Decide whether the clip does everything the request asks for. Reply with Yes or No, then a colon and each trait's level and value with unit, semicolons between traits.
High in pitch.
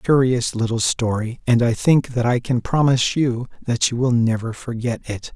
No: low, 120 Hz